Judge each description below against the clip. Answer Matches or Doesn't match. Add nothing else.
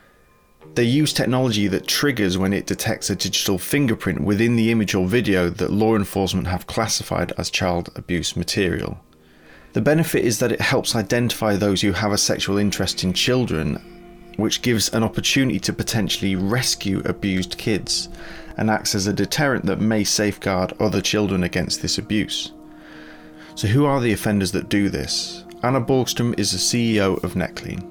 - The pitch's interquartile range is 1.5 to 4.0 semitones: Doesn't match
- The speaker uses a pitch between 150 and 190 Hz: Doesn't match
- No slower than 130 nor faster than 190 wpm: Matches